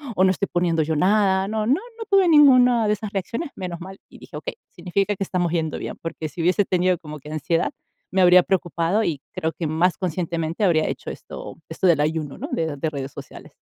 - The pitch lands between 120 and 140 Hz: No, medium, 180 Hz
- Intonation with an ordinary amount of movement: Yes, average, 3.6 semitones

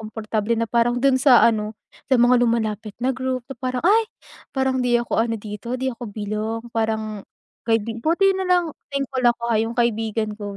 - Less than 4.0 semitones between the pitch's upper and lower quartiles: Yes, average, 2.9 semitones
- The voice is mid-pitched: No, high, 235 Hz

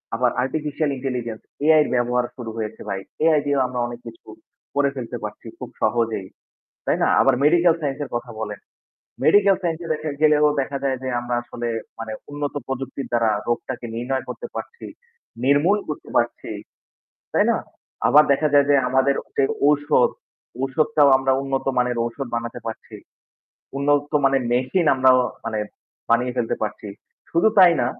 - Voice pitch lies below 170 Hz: Yes, low, 135 Hz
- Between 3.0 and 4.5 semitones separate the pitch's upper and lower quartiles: Yes, average, 3.4 semitones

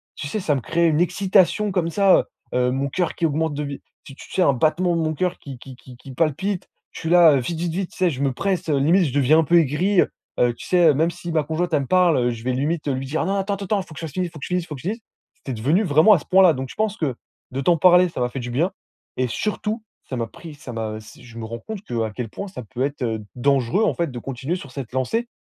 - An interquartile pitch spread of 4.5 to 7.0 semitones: Yes, wide, 5.5 semitones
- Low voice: No, medium, 155 Hz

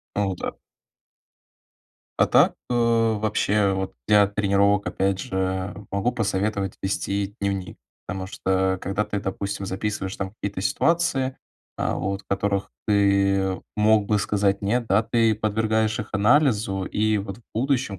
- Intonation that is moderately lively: No, narrow, 1.9 semitones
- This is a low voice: Yes, low, 100 Hz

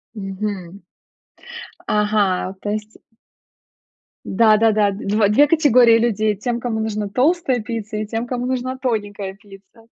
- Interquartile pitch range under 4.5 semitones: Yes, average, 2.8 semitones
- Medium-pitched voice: No, high, 215 Hz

